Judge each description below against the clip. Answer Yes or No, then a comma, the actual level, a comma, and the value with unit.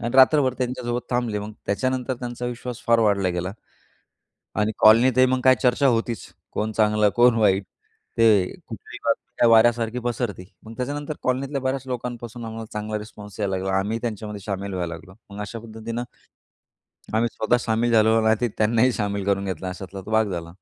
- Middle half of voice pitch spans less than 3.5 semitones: Yes, average, 2.9 semitones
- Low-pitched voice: Yes, low, 110 Hz